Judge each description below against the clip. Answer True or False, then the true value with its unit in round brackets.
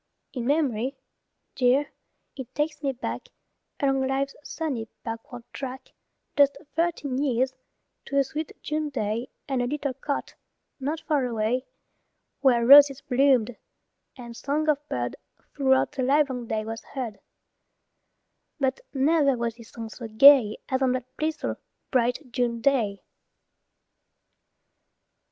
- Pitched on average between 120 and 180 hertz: False (265 Hz)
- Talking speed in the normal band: False (130 wpm)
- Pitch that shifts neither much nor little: True (3.1 semitones)